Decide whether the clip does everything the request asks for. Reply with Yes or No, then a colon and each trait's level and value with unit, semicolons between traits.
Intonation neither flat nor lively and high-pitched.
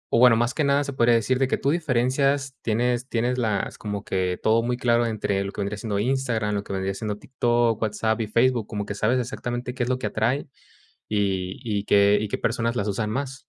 No: average, 3.4 semitones; low, 115 Hz